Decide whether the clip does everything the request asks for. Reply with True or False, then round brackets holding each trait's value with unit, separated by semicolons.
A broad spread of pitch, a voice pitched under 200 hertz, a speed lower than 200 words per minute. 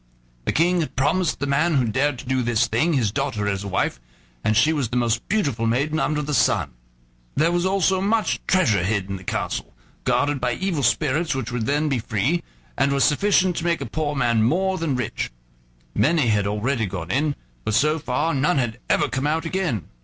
False (5.8 semitones; 140 Hz; 205 wpm)